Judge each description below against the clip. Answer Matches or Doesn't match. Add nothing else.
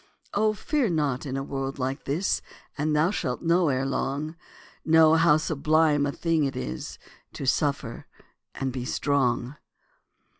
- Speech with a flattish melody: Doesn't match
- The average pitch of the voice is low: Doesn't match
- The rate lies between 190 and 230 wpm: Doesn't match